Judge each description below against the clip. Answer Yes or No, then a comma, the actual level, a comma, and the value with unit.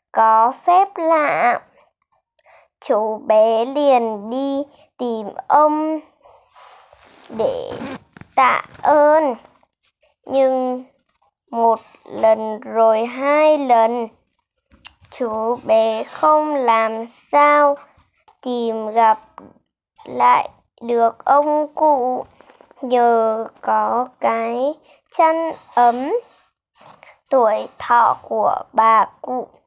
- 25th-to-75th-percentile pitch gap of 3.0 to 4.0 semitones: No, average, 4.8 semitones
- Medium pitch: No, very high, 250 Hz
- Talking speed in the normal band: No, slow, 80 wpm